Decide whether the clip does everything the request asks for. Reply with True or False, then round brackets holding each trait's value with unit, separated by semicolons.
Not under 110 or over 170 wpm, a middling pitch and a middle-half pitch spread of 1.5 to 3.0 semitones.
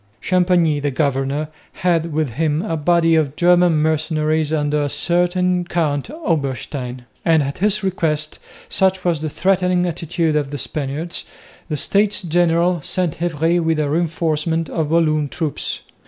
True (145 wpm; 160 Hz; 2.7 semitones)